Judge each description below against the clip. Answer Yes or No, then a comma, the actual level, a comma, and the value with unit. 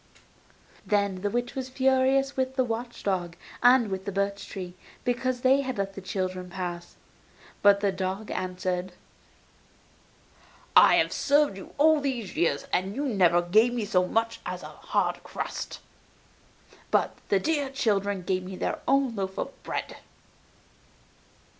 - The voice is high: Yes, high, 205 Hz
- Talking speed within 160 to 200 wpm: No, average, 150 wpm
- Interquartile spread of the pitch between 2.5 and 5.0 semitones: No, wide, 5.5 semitones